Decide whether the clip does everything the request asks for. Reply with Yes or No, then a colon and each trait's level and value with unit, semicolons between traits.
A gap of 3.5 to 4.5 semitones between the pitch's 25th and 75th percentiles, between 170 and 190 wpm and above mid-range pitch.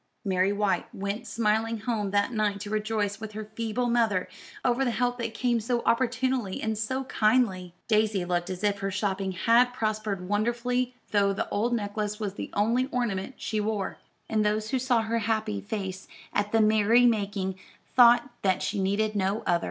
No: average, 2.7 semitones; average, 180 wpm; high, 215 Hz